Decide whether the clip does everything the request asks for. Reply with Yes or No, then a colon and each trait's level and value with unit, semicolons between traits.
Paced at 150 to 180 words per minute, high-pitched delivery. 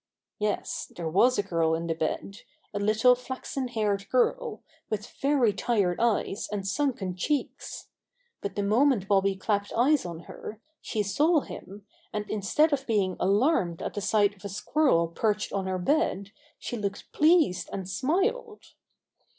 Yes: average, 160 wpm; high, 210 Hz